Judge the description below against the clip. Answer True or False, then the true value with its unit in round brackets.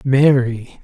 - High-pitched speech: False (130 Hz)